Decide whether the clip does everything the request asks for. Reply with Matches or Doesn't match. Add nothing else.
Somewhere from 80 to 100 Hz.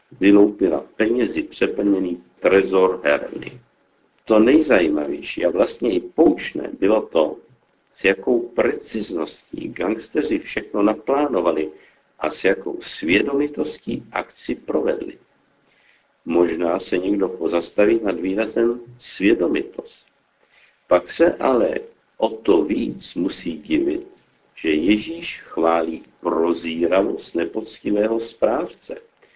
Doesn't match